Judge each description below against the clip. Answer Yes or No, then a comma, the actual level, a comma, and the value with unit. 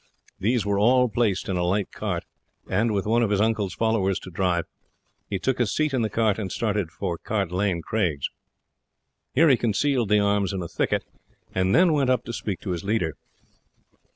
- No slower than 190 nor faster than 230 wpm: Yes, average, 200 wpm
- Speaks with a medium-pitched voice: No, low, 105 Hz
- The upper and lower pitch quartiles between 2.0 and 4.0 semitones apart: Yes, average, 3.7 semitones